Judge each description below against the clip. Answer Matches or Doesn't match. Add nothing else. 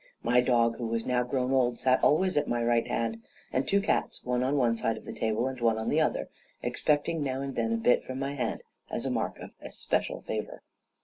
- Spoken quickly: Matches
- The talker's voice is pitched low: Matches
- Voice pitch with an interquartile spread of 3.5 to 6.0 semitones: Doesn't match